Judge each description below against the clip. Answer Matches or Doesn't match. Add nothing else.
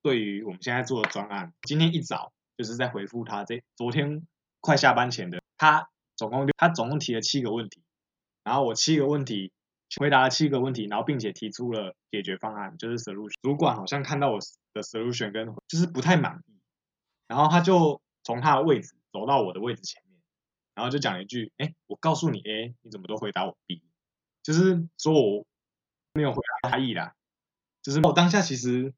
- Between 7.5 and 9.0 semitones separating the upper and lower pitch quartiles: Doesn't match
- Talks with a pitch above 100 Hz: Matches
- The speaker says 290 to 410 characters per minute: Matches